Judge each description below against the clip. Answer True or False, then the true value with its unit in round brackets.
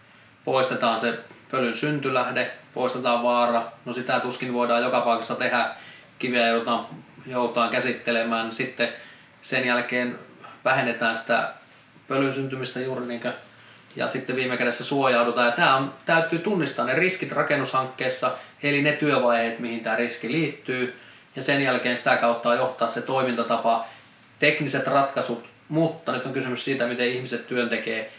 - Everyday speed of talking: True (130 wpm)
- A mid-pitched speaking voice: False (125 Hz)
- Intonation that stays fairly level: True (1.8 semitones)